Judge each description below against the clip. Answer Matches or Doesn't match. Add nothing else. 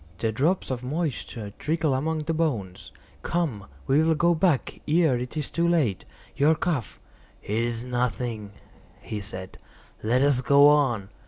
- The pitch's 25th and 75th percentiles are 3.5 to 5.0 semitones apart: Doesn't match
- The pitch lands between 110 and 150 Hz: Matches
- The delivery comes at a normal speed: Matches